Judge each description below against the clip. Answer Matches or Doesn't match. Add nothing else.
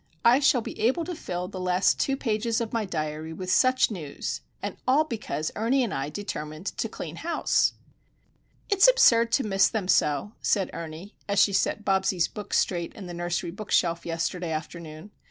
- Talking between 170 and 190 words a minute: Matches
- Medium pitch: Doesn't match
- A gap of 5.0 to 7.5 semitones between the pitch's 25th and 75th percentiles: Matches